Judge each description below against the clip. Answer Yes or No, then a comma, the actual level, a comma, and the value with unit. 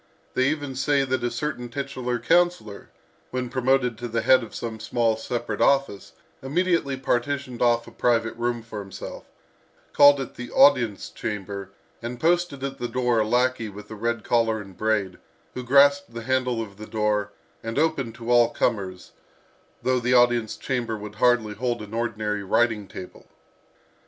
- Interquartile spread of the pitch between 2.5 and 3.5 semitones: Yes, average, 2.9 semitones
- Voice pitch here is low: Yes, low, 120 Hz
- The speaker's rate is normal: Yes, average, 165 wpm